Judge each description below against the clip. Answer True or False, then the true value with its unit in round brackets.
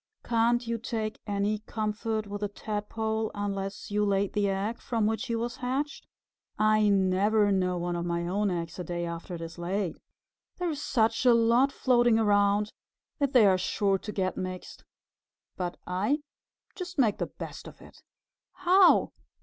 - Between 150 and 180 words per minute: True (170 wpm)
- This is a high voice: True (210 Hz)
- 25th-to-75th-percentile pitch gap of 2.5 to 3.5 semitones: True (3.1 semitones)